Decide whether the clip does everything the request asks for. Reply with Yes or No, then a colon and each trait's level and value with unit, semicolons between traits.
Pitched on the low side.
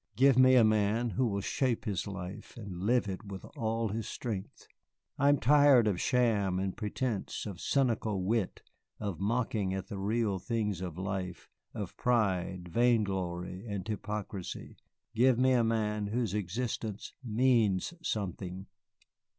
Yes: low, 105 Hz